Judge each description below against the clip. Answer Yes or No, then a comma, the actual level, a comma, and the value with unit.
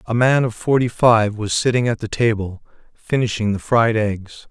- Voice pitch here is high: No, low, 110 Hz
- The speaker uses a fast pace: No, average, 185 wpm